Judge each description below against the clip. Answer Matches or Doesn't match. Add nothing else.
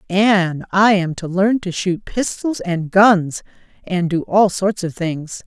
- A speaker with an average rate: Matches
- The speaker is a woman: Matches